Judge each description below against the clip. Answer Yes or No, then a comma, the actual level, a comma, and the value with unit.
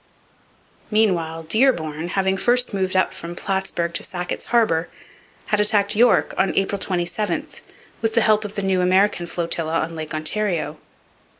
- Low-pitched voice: No, high, 190 Hz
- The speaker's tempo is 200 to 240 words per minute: No, average, 145 wpm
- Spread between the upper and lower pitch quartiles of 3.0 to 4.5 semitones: Yes, average, 3.8 semitones